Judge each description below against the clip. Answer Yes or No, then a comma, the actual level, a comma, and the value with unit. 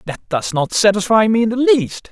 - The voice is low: No, high, 210 Hz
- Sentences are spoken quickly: Yes, fast, 225 wpm